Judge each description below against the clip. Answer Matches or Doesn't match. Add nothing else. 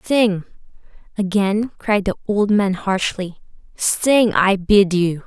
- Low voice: Doesn't match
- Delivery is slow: Matches